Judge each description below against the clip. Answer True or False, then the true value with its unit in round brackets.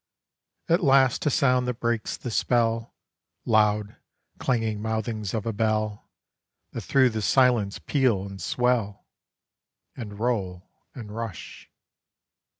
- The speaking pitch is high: False (115 Hz)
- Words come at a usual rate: False (120 wpm)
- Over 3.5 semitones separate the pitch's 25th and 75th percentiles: False (2.9 semitones)